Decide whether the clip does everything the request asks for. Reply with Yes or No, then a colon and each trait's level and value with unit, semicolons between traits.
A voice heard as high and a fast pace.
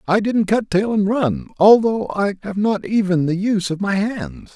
Yes: high, 195 Hz; fast, 210 wpm